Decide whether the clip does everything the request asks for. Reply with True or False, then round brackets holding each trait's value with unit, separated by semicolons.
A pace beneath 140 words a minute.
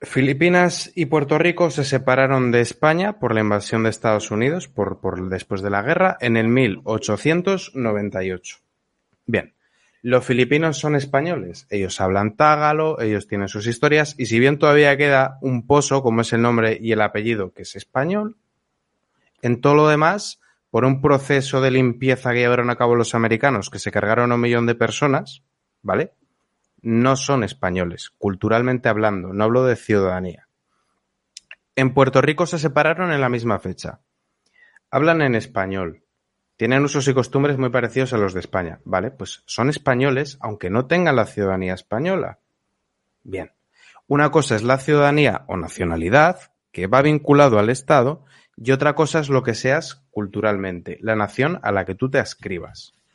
False (165 wpm)